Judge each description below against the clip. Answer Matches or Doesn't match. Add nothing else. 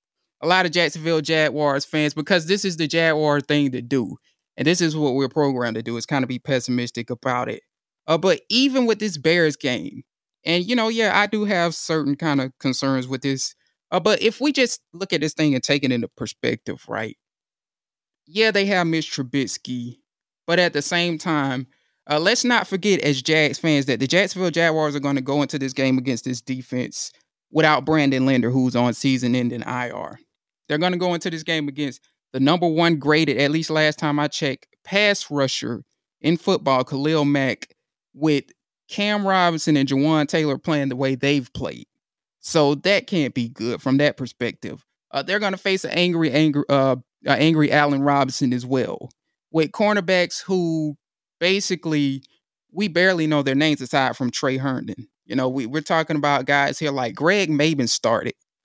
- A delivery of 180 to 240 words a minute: Matches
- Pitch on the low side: Doesn't match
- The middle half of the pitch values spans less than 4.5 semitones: Matches